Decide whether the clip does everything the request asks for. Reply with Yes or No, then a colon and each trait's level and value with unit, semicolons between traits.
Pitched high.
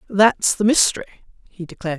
Yes: high, 195 Hz